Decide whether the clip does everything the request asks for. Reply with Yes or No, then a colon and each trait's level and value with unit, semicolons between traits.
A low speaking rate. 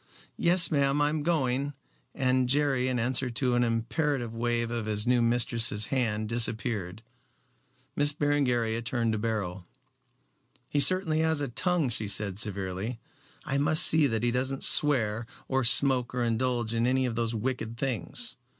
No: average, 160 wpm